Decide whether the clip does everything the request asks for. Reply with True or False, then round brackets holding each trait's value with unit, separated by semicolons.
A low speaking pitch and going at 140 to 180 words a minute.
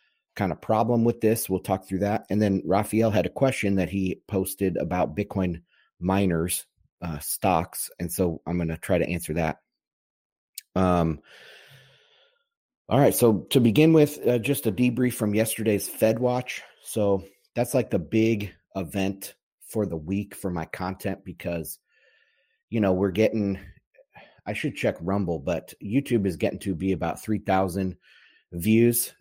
True (100 Hz; 160 wpm)